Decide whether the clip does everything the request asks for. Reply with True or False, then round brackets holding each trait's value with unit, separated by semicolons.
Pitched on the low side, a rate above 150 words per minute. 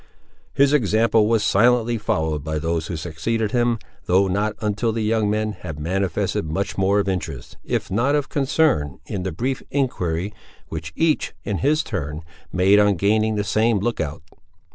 True (105 Hz; 170 wpm)